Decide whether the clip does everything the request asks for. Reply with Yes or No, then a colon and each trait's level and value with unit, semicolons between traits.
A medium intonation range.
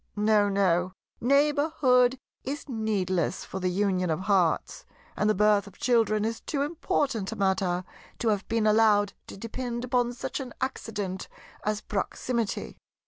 Yes: average, 4.1 semitones